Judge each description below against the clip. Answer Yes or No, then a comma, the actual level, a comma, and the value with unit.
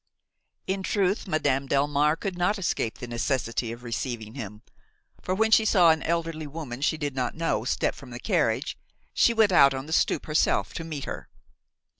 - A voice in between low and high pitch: Yes, medium, 150 Hz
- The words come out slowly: No, average, 185 wpm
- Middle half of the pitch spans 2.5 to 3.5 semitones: No, average, 5.3 semitones